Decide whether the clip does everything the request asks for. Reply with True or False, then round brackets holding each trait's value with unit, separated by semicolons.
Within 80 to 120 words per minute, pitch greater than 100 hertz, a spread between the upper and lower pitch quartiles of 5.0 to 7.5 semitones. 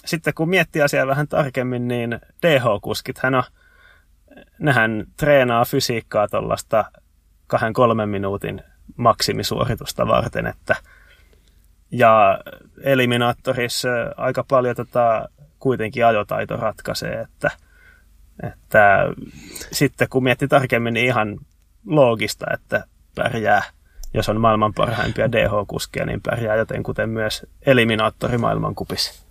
False (110 wpm; 120 Hz; 3.8 semitones)